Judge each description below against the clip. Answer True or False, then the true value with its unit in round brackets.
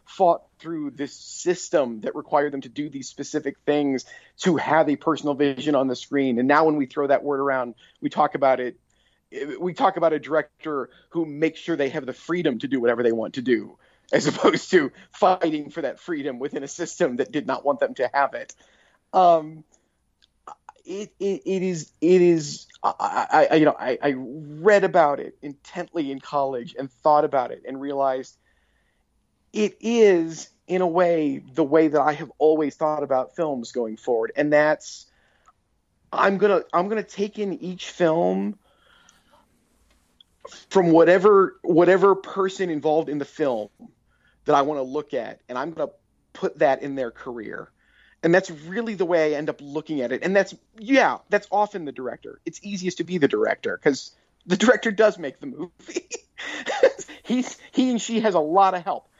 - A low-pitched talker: False (155 Hz)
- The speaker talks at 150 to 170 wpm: False (190 wpm)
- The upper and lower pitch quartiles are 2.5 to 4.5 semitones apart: False (5.1 semitones)